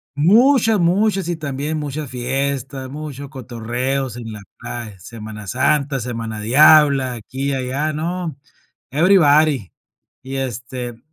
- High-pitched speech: No, low, 135 Hz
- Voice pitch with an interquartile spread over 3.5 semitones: Yes, average, 3.9 semitones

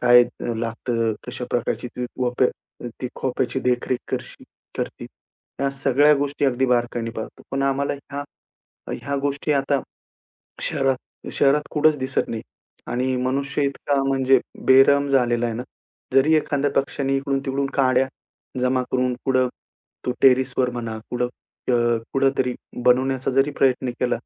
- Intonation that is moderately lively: No, narrow, 1.9 semitones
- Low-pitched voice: Yes, low, 130 Hz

